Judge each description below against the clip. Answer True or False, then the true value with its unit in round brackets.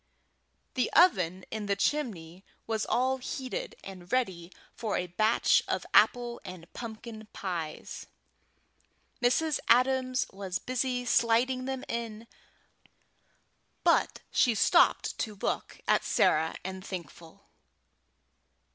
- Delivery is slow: True (110 wpm)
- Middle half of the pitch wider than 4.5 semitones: True (5.2 semitones)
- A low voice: False (225 Hz)